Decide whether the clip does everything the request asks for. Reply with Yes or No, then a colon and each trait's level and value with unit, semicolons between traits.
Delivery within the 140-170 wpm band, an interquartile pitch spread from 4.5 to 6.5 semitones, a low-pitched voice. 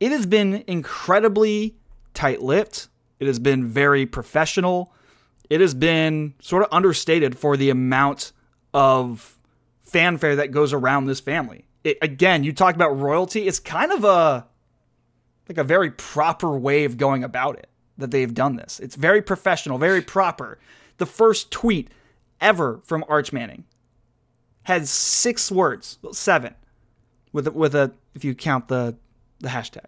No: average, 150 wpm; wide, 5.6 semitones; medium, 145 Hz